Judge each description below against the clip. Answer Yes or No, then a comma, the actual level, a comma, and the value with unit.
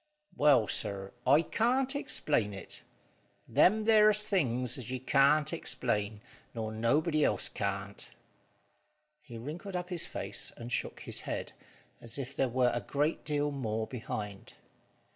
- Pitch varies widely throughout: Yes, wide, 5.9 semitones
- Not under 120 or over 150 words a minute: Yes, average, 140 wpm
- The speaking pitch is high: No, low, 135 Hz